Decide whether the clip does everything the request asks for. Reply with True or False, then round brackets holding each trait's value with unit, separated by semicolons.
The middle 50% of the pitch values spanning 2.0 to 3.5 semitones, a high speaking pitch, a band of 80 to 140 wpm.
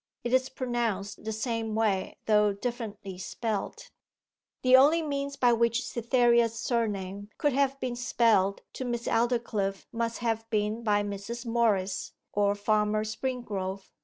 True (2.8 semitones; 225 Hz; 135 wpm)